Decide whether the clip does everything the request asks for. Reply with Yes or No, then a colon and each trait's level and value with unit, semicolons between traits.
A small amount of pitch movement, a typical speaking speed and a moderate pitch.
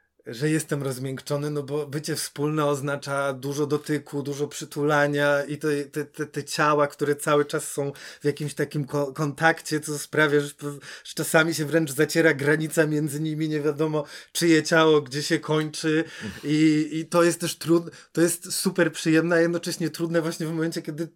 No: narrow, 1.7 semitones; fast, 165 wpm; medium, 150 Hz